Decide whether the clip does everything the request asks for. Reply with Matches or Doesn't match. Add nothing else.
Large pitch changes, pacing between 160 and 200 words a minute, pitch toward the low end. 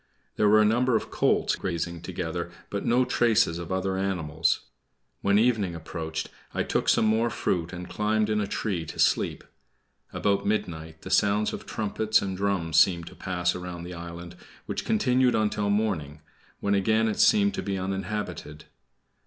Doesn't match